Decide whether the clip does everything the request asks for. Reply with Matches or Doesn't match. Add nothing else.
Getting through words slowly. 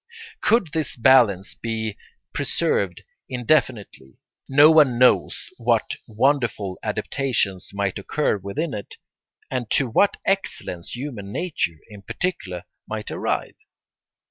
Matches